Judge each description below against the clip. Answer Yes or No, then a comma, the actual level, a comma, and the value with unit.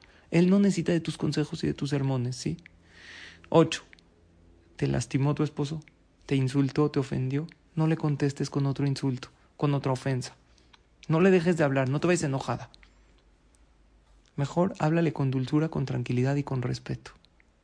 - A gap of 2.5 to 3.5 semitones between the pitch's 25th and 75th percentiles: No, average, 3.9 semitones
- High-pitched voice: No, medium, 140 Hz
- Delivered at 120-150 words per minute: No, average, 160 wpm